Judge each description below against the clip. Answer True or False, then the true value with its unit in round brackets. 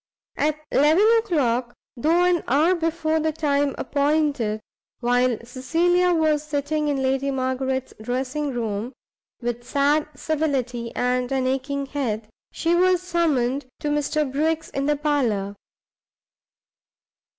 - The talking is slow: True (120 wpm)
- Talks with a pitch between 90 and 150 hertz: False (280 Hz)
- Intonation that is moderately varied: True (3.6 semitones)